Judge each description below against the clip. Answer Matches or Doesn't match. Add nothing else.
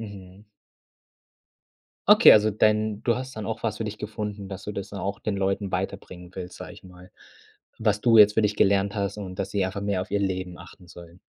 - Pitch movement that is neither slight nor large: Doesn't match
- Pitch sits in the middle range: Doesn't match